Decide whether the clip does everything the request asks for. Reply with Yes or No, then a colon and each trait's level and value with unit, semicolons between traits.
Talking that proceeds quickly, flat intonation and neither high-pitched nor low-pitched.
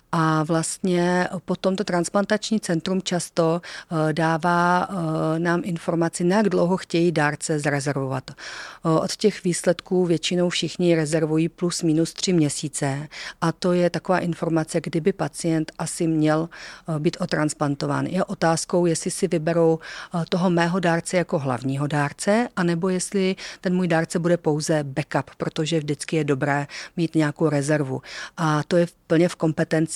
No: average, 135 wpm; narrow, 2.2 semitones; medium, 170 Hz